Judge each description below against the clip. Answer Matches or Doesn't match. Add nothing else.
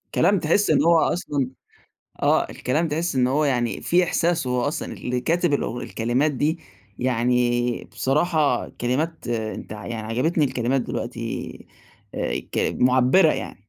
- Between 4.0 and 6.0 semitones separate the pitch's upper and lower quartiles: Matches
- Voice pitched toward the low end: Matches